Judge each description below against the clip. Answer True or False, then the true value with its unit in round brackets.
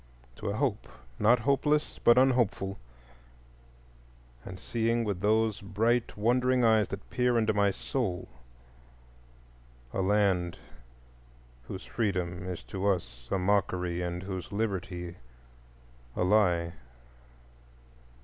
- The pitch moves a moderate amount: True (4.0 semitones)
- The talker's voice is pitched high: False (100 Hz)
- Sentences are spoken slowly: True (110 wpm)